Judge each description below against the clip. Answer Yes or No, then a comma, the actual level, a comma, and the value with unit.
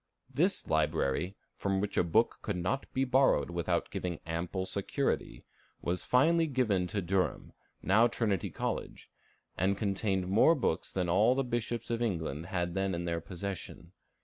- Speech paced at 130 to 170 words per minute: Yes, average, 155 wpm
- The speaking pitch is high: No, very low, 95 Hz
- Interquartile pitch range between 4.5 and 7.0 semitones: Yes, average, 4.9 semitones